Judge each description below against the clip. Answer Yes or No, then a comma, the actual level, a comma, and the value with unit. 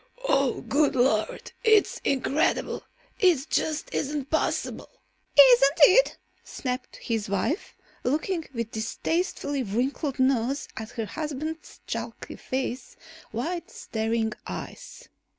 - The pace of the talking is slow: Yes, slow, 105 wpm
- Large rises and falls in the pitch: No, average, 4.8 semitones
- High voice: Yes, very high, 270 Hz